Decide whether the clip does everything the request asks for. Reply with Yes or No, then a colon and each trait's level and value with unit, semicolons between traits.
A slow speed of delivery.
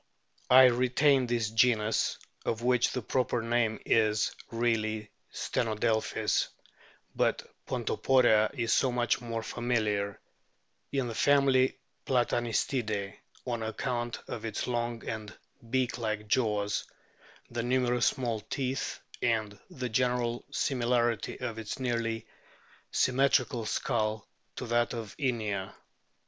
Yes: slow, 110 wpm